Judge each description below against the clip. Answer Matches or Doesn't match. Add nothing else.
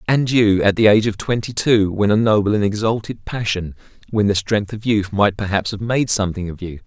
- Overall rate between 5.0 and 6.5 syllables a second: Matches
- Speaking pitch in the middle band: Doesn't match